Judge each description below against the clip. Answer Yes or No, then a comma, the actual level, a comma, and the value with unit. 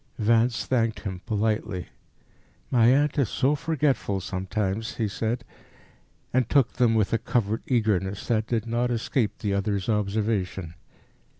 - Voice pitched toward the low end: Yes, low, 110 Hz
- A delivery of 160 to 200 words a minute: No, slow, 135 wpm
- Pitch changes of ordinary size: Yes, average, 3.1 semitones